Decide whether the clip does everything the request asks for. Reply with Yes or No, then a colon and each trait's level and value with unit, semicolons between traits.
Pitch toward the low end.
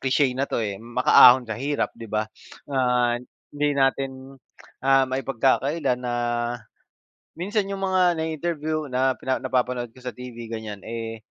Yes: low, 130 Hz